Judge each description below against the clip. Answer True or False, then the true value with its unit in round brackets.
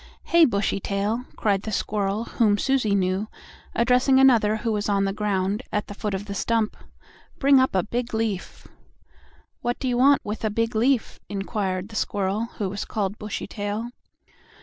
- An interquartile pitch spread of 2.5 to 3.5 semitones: True (2.8 semitones)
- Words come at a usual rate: True (170 wpm)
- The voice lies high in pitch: True (210 Hz)